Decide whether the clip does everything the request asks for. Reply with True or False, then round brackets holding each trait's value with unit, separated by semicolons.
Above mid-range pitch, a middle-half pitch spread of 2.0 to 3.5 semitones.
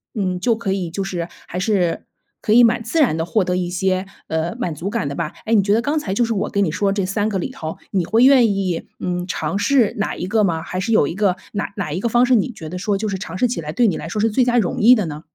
False (195 Hz; 4.0 semitones)